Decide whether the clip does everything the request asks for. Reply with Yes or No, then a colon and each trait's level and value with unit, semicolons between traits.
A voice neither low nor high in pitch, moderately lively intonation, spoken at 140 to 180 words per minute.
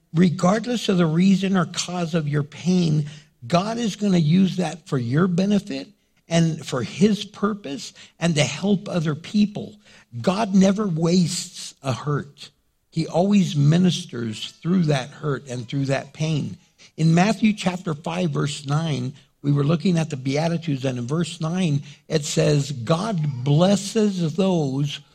Yes: medium, 165 Hz; average, 4.0 semitones; average, 150 wpm